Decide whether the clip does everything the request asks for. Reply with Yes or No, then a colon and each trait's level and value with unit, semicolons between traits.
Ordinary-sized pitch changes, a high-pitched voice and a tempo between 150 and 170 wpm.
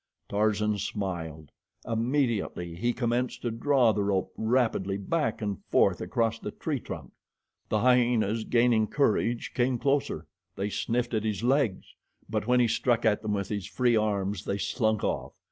No: average, 3.2 semitones; low, 110 Hz; average, 160 wpm